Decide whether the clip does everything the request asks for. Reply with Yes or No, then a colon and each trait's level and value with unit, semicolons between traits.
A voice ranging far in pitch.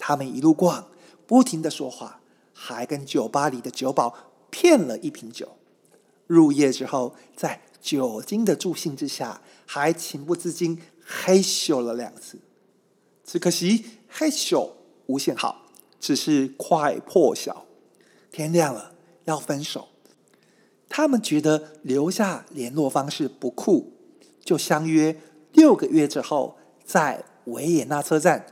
No: average, 4.6 semitones